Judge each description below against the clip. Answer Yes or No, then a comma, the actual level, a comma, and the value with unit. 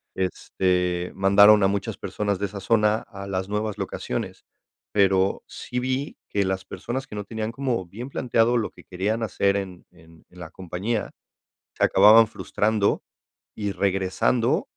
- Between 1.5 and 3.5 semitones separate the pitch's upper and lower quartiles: Yes, average, 2.9 semitones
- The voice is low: Yes, low, 100 Hz